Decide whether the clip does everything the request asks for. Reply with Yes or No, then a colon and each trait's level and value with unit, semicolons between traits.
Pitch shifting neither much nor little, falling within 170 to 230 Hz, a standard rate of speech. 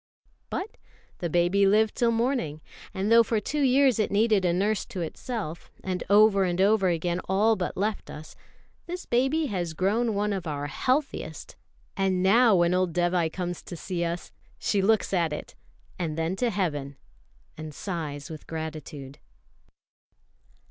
Yes: average, 4.5 semitones; high, 190 Hz; average, 160 wpm